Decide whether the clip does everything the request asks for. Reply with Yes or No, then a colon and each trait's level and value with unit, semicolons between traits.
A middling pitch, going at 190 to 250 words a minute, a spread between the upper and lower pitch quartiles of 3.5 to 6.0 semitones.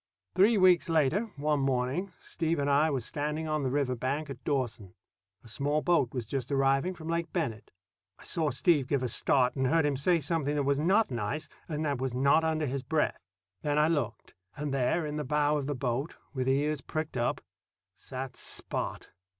No: medium, 145 Hz; average, 200 wpm; average, 3.1 semitones